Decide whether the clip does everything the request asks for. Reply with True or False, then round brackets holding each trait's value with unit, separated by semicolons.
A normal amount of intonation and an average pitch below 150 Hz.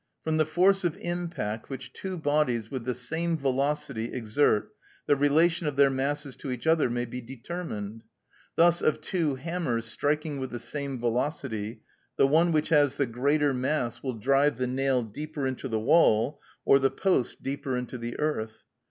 True (3.9 semitones; 140 Hz)